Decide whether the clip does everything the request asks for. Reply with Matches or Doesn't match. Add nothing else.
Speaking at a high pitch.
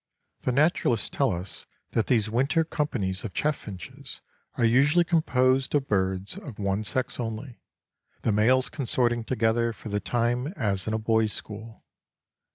Doesn't match